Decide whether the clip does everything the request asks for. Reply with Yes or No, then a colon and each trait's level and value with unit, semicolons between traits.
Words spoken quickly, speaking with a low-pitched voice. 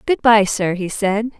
No: fast, 215 wpm; high, 210 Hz